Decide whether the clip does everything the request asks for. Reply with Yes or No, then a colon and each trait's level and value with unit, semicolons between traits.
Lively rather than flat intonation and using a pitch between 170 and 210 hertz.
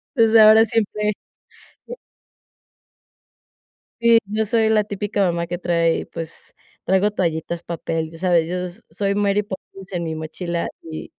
No: average, 3.8 semitones; high, 190 Hz